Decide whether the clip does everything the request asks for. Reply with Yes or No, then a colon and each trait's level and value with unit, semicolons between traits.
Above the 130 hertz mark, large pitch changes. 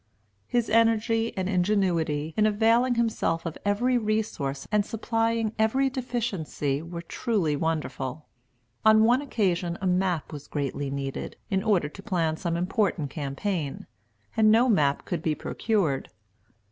Yes: high, 190 Hz; wide, 6.0 semitones